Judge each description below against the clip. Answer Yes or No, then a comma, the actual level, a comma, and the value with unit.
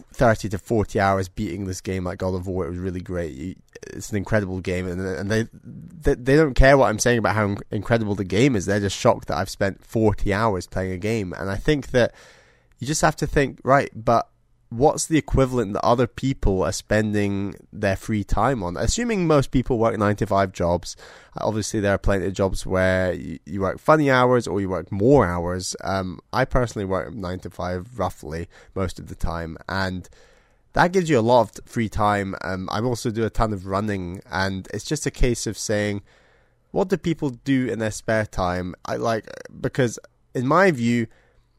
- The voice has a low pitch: Yes, low, 105 Hz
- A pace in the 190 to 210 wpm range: Yes, fast, 205 wpm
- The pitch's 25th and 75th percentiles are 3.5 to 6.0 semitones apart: Yes, average, 4.4 semitones